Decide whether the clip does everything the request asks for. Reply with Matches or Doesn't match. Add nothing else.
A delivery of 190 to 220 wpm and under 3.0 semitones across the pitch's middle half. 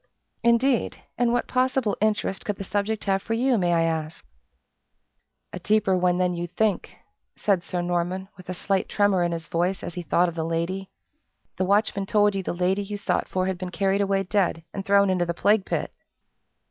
Matches